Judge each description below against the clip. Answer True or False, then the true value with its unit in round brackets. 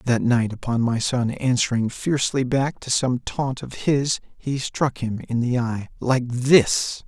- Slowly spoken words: False (180 wpm)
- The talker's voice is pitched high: False (125 Hz)